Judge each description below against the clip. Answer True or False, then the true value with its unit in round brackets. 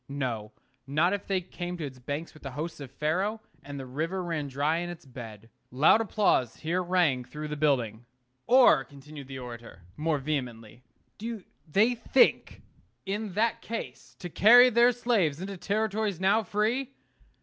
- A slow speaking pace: False (165 wpm)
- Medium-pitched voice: True (160 Hz)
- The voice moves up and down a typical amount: False (7.0 semitones)